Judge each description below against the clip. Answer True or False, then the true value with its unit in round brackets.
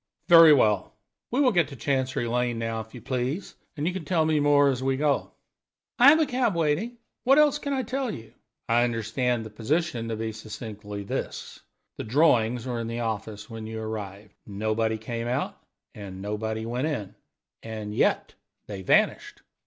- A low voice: True (120 Hz)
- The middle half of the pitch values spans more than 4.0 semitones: True (5.6 semitones)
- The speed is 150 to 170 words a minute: False (185 wpm)